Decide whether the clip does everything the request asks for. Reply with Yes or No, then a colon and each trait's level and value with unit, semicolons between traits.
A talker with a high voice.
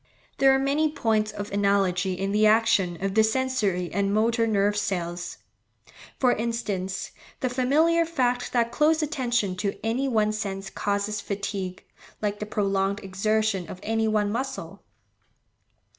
Yes: high, 215 Hz